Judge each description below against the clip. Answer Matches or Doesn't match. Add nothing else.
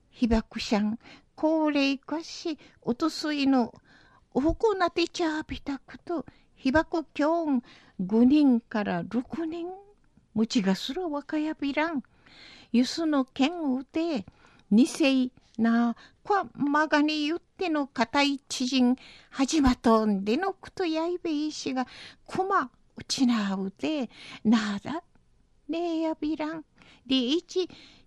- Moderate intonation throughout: Matches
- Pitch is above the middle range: Matches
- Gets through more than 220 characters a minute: Doesn't match